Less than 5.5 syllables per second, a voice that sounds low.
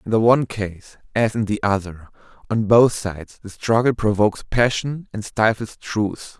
Yes: 4.7 syllables/s; low, 110 Hz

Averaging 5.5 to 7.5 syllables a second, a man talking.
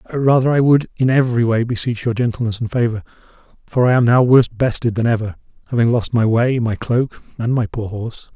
Yes: 5.9 syllables/s; male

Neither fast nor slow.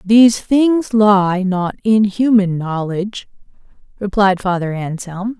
No: slow, 110 wpm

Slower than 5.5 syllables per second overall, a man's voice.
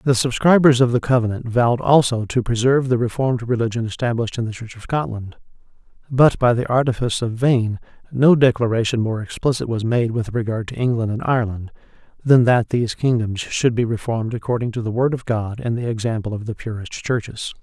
No: 5.9 syllables/s; male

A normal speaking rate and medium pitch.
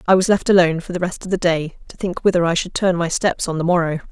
No: fast, 305 wpm; medium, 175 Hz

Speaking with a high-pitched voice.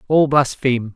No: low, 130 Hz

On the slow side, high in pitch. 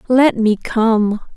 Yes: slow, 130 wpm; high, 225 Hz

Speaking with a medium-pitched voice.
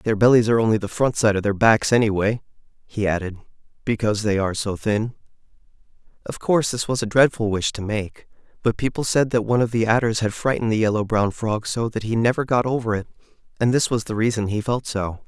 No: low, 110 Hz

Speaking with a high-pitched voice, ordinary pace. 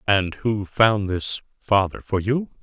No: low, 105 Hz; average, 160 wpm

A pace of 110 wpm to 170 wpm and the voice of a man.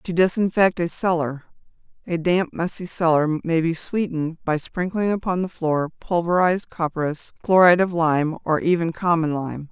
No: average, 150 wpm; female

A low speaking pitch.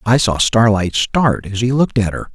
Yes: low, 110 Hz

